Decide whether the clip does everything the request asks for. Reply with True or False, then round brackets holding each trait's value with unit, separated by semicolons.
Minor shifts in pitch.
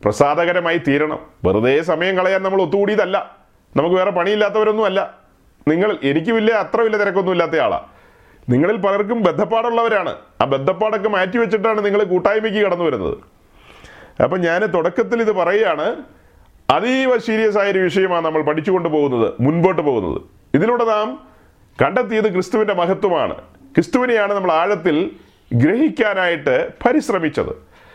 False (3.7 semitones)